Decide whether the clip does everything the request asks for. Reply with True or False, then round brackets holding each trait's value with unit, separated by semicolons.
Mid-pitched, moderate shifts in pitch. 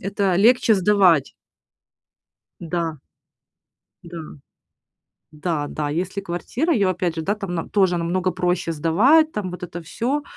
True (180 Hz; 3.2 semitones)